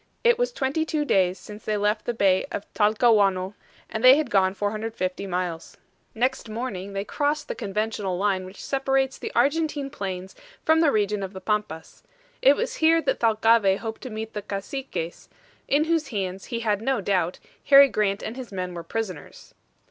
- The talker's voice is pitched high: Yes, high, 215 Hz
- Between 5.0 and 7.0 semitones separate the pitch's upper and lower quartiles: Yes, wide, 5.6 semitones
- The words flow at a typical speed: Yes, average, 180 wpm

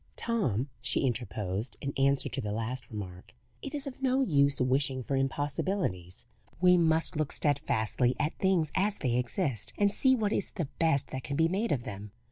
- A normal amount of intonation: No, wide, 6.9 semitones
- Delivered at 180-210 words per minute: Yes, average, 185 wpm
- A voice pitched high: No, medium, 140 Hz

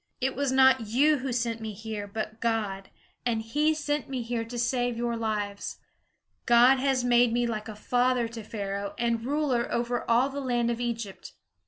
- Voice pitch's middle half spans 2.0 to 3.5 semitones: Yes, narrow, 2.4 semitones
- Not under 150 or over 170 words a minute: No, average, 180 wpm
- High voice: Yes, high, 235 Hz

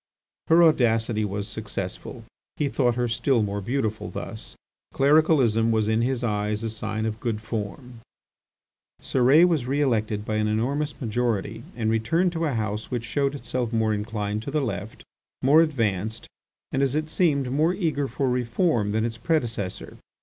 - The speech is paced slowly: No, average, 165 wpm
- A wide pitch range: No, average, 4.3 semitones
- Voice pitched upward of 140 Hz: No, low, 115 Hz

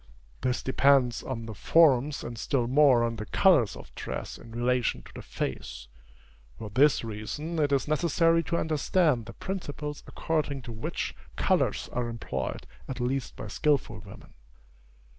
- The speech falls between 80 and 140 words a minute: No, average, 155 wpm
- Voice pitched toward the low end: Yes, low, 130 Hz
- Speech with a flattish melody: No, average, 4.5 semitones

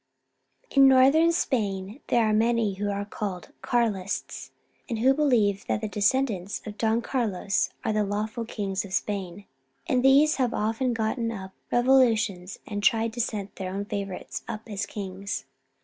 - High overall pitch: Yes, high, 215 Hz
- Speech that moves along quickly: No, average, 165 wpm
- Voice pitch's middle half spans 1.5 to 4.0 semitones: Yes, average, 3.2 semitones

